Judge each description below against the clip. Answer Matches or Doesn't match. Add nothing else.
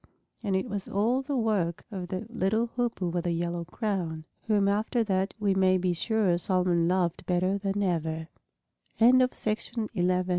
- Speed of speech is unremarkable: Matches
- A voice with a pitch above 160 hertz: Matches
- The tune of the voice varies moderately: Matches